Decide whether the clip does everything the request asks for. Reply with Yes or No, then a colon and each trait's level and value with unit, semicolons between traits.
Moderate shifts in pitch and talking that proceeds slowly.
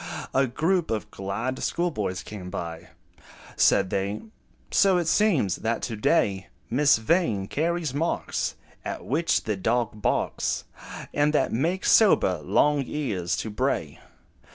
No: wide, 8.2 semitones; slow, 130 wpm